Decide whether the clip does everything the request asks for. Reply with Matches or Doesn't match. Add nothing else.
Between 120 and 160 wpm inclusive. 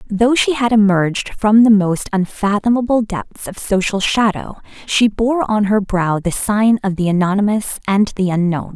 Doesn't match